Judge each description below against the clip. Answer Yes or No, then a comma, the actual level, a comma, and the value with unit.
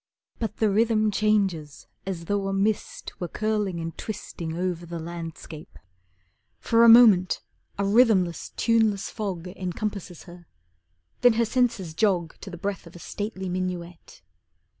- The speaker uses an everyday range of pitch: Yes, average, 3.8 semitones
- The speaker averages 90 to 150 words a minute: Yes, average, 140 wpm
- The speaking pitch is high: Yes, high, 195 Hz